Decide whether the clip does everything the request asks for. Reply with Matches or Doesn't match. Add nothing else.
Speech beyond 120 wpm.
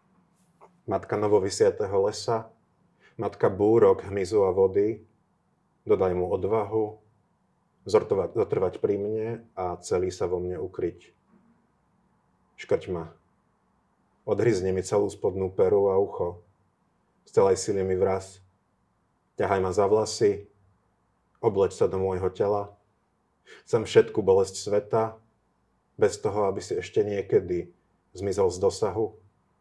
Doesn't match